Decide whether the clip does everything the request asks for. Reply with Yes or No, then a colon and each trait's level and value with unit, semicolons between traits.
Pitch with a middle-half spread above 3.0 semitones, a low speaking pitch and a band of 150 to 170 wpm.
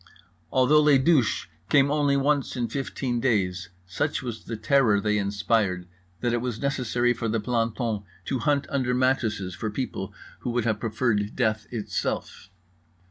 Yes: average, 3.8 semitones; low, 120 Hz; average, 155 wpm